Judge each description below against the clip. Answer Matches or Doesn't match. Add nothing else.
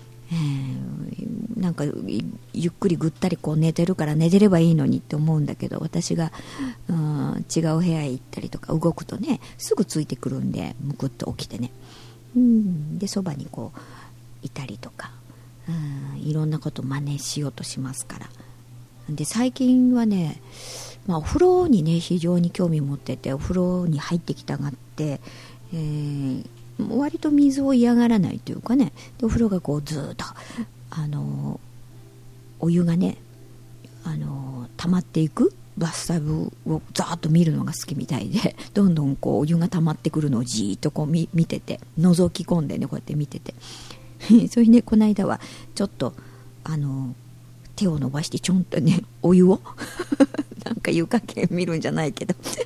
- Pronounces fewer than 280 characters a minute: Doesn't match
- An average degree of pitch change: Doesn't match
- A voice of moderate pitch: Matches